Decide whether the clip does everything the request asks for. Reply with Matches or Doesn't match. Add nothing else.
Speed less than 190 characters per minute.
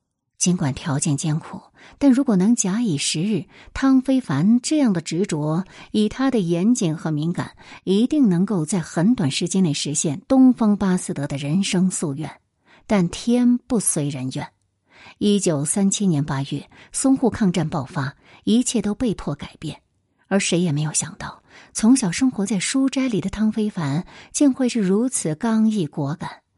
Doesn't match